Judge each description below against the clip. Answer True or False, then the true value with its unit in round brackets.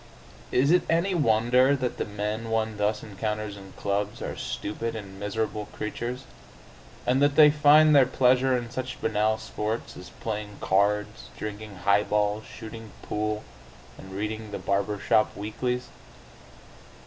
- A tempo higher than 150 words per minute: False (140 wpm)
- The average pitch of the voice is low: True (110 Hz)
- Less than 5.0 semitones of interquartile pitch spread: True (3.2 semitones)